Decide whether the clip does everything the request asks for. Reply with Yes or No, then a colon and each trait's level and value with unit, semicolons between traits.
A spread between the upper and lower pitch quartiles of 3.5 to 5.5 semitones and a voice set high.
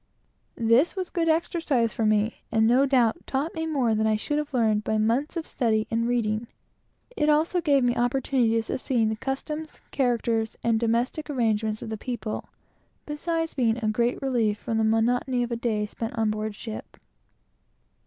Yes: average, 3.8 semitones; high, 235 Hz